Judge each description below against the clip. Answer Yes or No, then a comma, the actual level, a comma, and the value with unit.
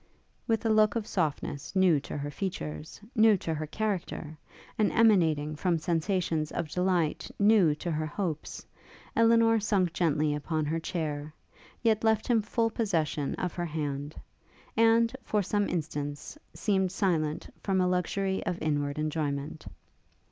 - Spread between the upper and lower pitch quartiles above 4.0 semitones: Yes, average, 5.3 semitones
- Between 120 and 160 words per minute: Yes, average, 145 wpm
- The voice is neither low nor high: Yes, medium, 175 Hz